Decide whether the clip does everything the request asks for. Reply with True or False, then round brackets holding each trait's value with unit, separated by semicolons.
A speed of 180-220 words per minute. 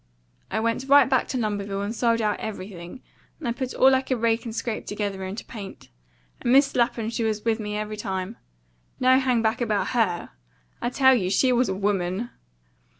True (190 wpm)